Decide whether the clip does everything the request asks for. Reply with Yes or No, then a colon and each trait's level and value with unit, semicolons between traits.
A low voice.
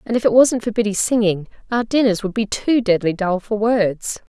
No: high, 215 Hz